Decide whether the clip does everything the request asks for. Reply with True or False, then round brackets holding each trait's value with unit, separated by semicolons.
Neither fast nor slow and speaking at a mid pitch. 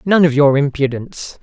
True (170 wpm; 145 Hz)